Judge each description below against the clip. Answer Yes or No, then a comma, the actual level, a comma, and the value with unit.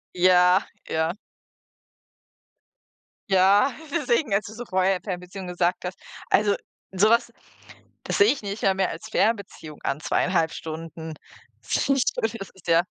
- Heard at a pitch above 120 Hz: Yes, high, 190 Hz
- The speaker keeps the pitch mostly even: No, average, 3.3 semitones